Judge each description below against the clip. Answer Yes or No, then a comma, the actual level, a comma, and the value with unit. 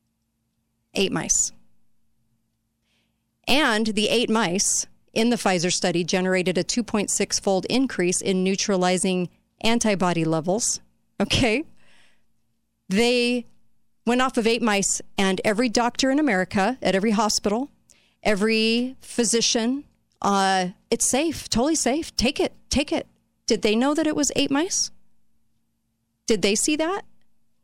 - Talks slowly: Yes, slow, 125 wpm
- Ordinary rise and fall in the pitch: Yes, average, 5.0 semitones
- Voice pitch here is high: Yes, high, 215 Hz